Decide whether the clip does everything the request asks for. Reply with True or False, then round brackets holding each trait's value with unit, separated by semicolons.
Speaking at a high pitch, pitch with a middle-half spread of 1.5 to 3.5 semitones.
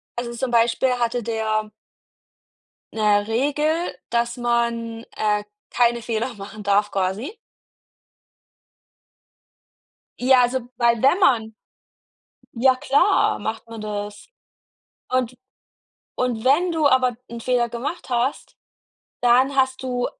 True (240 Hz; 2.6 semitones)